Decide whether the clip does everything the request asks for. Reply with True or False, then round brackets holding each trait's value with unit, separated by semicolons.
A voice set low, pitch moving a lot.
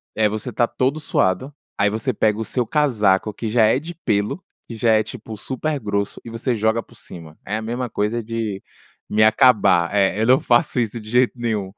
False (110 Hz; 2.9 semitones)